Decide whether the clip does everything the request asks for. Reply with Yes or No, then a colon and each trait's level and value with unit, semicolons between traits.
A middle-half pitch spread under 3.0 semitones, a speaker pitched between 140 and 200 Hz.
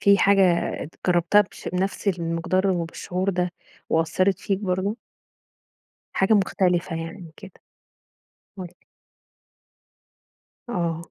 Yes: narrow, 2.5 semitones; medium, 185 Hz